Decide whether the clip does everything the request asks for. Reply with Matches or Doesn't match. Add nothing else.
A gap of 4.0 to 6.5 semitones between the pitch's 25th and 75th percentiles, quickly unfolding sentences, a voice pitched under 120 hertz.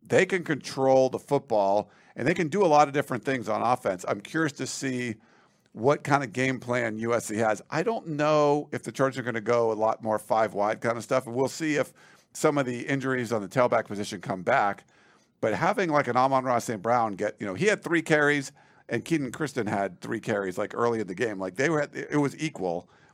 Doesn't match